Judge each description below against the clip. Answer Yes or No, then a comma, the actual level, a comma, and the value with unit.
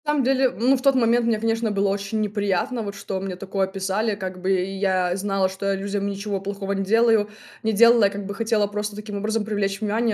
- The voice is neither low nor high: No, high, 205 Hz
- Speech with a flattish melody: Yes, narrow, 2.3 semitones